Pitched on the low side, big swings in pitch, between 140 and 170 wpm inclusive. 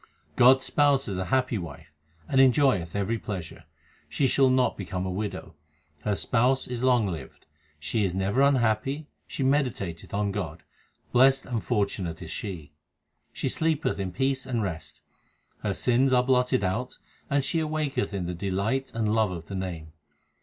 Yes: low, 110 Hz; wide, 5.9 semitones; average, 165 wpm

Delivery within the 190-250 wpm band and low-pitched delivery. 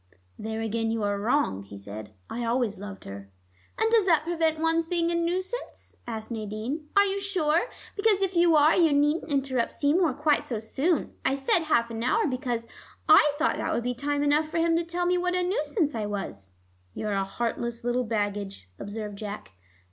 No: average, 200 wpm; very high, 270 Hz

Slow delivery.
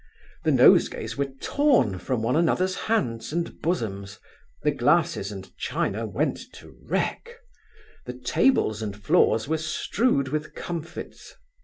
Yes: slow, 130 wpm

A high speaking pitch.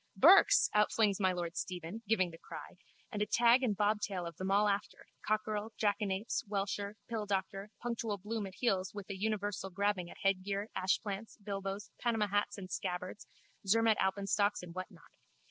Yes: high, 200 Hz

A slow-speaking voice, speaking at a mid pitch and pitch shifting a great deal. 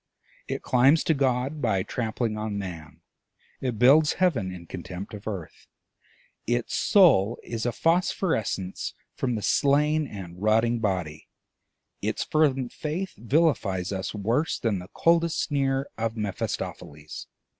No: slow, 130 wpm; low, 115 Hz; wide, 6.8 semitones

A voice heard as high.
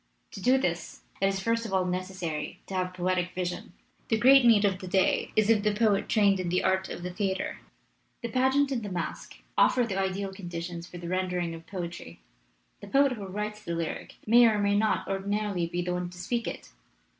Yes: high, 195 Hz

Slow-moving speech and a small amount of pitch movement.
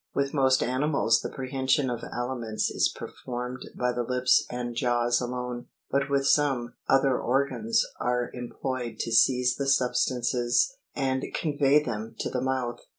No: average, 150 wpm; narrow, 1.8 semitones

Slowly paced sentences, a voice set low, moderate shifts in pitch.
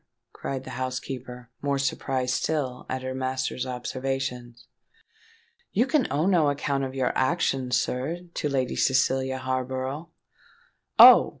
No: slow, 125 wpm; low, 130 Hz; narrow, 1.4 semitones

